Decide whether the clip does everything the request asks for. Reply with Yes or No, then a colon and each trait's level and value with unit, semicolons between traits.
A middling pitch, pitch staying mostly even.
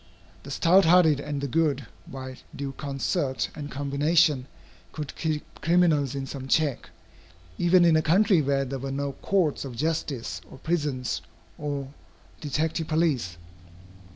No: medium, 145 Hz; average, 3.0 semitones